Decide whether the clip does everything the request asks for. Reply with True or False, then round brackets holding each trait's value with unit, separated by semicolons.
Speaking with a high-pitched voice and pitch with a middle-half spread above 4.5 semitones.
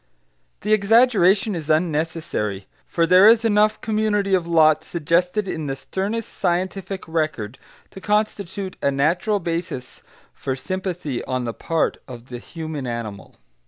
False (170 Hz; 5.2 semitones)